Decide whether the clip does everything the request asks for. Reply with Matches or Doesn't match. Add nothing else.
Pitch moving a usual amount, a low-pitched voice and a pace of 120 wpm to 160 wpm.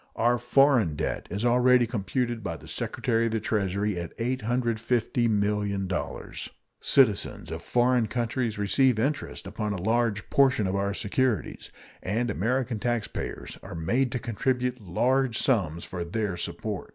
Matches